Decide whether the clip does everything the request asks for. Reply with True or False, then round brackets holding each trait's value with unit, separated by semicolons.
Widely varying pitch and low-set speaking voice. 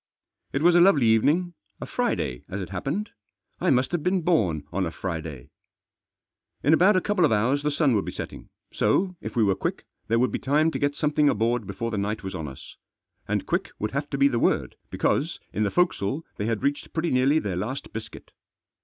True (7.1 semitones; 130 Hz)